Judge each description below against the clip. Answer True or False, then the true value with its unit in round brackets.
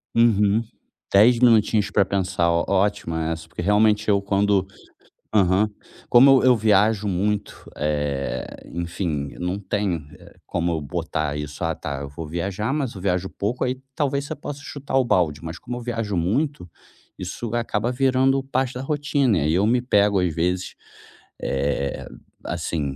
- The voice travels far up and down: True (5.9 semitones)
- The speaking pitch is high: False (100 Hz)